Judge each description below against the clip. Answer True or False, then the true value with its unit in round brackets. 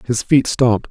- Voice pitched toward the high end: False (120 Hz)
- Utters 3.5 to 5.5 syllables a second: True (5.0 syllables/s)